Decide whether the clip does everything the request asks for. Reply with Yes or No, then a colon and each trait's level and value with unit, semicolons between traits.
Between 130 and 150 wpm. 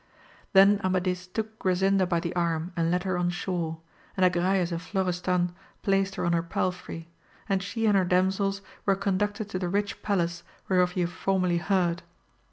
No: average, 175 wpm